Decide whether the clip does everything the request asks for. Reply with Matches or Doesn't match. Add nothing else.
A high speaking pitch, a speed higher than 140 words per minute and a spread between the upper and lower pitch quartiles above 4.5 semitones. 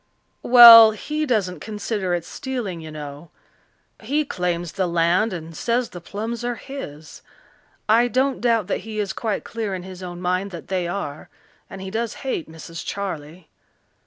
Matches